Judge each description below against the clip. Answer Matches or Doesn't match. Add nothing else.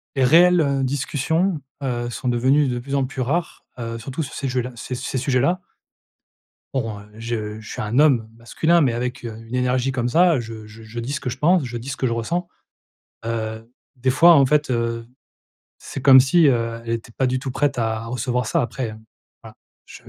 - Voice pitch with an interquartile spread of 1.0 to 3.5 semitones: Matches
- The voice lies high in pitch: Doesn't match